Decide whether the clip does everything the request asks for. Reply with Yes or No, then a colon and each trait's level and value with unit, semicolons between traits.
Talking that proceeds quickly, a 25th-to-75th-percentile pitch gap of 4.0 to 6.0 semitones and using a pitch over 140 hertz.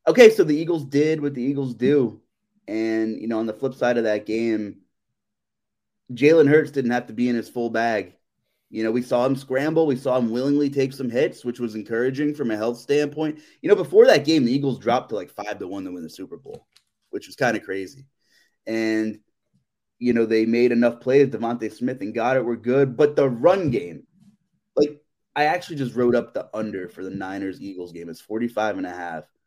No: fast, 220 wpm; average, 4.5 semitones; low, 125 Hz